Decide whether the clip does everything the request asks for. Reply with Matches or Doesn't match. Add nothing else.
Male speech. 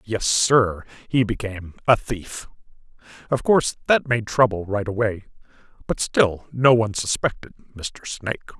Matches